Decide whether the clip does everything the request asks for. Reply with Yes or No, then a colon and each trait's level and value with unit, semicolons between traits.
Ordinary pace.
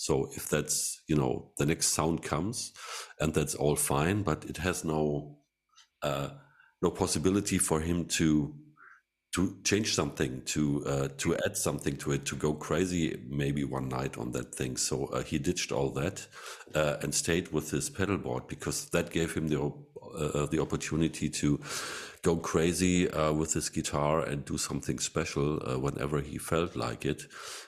Yes: average, 175 wpm